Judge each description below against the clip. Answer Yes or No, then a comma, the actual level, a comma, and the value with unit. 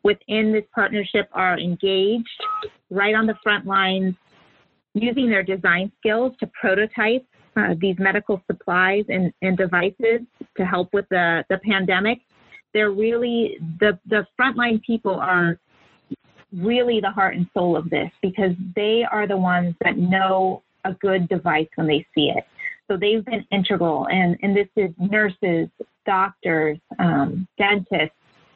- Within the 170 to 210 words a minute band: No, average, 145 wpm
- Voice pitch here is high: Yes, high, 195 Hz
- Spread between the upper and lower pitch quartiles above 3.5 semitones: No, average, 2.9 semitones